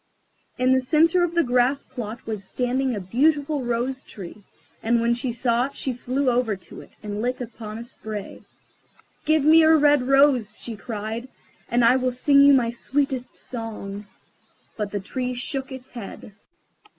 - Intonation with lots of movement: No, average, 3.2 semitones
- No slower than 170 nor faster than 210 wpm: Yes, average, 175 wpm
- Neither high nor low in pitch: No, very high, 250 Hz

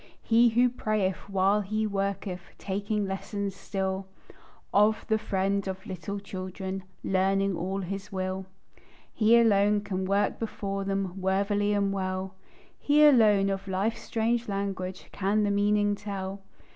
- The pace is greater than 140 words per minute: No, slow, 135 wpm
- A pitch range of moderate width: No, narrow, 1.5 semitones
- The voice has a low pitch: No, high, 195 Hz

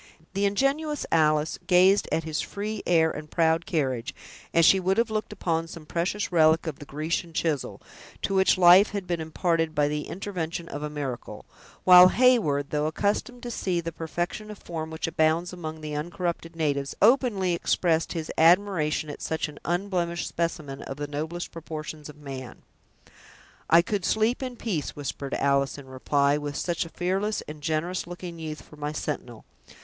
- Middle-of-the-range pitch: Yes, medium, 165 Hz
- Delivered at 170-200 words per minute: Yes, average, 175 wpm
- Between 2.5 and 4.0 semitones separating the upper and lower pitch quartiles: Yes, average, 3.4 semitones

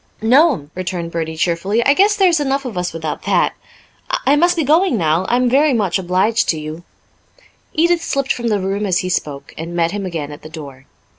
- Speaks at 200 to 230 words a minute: Yes, fast, 205 wpm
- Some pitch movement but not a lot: No, wide, 8.7 semitones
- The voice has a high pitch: Yes, high, 195 Hz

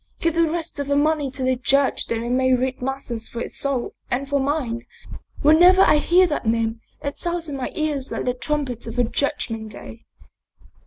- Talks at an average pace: No, fast, 210 wpm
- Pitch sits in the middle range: No, very high, 275 Hz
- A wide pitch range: No, average, 3.7 semitones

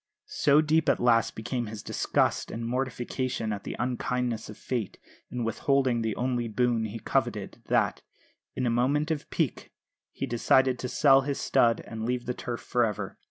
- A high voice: No, low, 120 Hz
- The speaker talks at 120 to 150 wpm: No, average, 175 wpm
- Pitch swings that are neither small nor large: No, narrow, 2.2 semitones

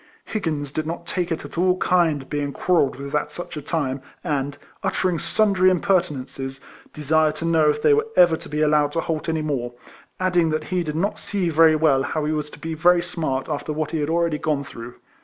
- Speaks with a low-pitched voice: No, medium, 155 Hz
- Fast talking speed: Yes, fast, 215 wpm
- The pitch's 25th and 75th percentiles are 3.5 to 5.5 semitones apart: No, average, 2.9 semitones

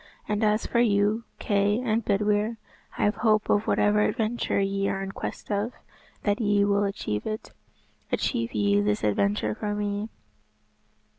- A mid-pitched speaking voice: No, high, 205 Hz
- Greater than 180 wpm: No, average, 155 wpm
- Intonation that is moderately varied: No, narrow, 1.4 semitones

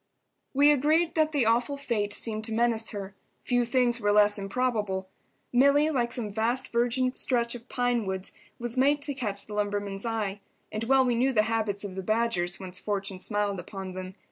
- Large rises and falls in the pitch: No, average, 3.7 semitones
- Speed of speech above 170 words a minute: Yes, average, 190 wpm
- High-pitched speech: Yes, high, 225 Hz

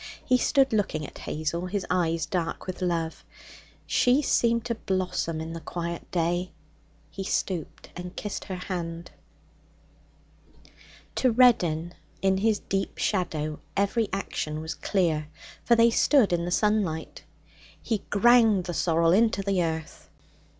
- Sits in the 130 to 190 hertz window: Yes, medium, 185 Hz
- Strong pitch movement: No, average, 4.2 semitones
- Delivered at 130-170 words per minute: Yes, slow, 135 wpm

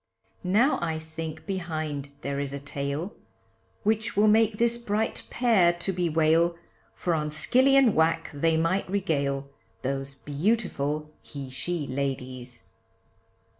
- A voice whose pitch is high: No, medium, 160 Hz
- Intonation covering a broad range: Yes, wide, 6.0 semitones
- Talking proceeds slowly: Yes, slow, 130 wpm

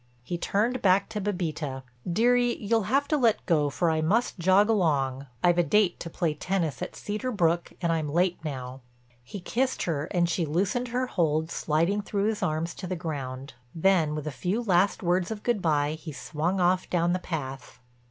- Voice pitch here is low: No, medium, 175 Hz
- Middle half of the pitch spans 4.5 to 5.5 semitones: Yes, average, 4.8 semitones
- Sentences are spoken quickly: No, average, 195 wpm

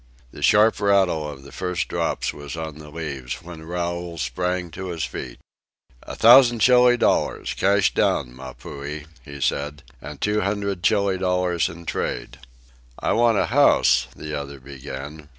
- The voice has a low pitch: Yes, very low, 85 Hz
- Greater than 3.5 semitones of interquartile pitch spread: Yes, average, 5.2 semitones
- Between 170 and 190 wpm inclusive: No, average, 160 wpm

